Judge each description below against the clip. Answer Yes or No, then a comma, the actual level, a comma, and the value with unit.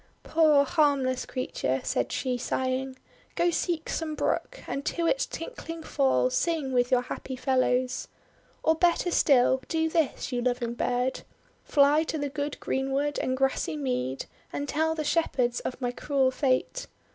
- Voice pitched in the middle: No, very high, 270 Hz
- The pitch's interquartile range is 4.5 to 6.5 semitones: No, average, 3.7 semitones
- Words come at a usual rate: Yes, average, 155 wpm